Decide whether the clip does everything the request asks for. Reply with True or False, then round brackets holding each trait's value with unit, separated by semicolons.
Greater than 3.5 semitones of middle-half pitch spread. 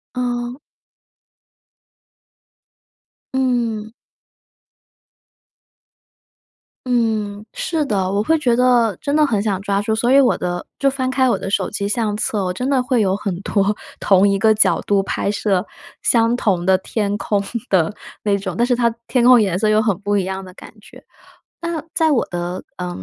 True (3.9 semitones)